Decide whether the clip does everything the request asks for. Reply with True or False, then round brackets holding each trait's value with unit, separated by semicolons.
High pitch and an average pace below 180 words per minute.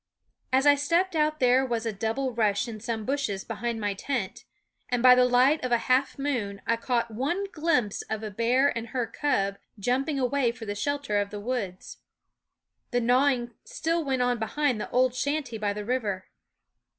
False (245 Hz; 185 wpm)